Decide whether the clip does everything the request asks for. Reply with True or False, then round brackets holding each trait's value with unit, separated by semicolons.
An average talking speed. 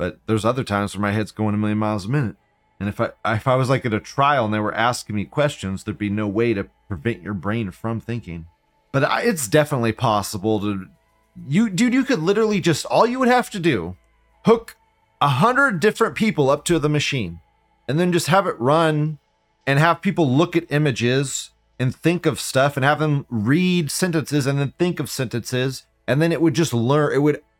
False (215 wpm)